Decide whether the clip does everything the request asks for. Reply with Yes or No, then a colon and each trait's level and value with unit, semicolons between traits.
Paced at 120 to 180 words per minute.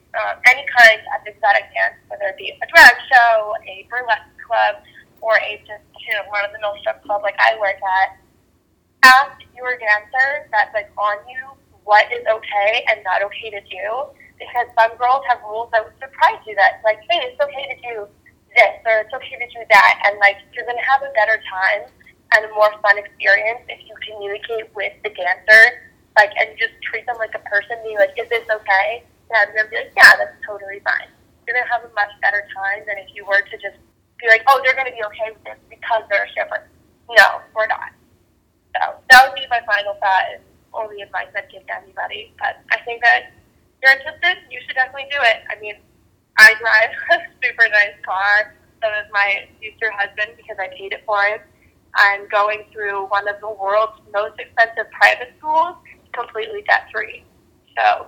No: fast, 205 wpm